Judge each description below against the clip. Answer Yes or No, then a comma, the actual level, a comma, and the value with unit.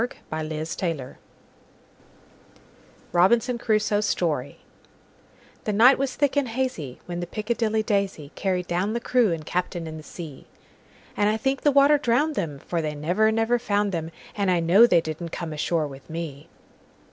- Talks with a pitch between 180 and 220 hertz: Yes, medium, 185 Hz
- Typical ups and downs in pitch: No, wide, 6.0 semitones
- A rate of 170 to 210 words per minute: No, average, 140 wpm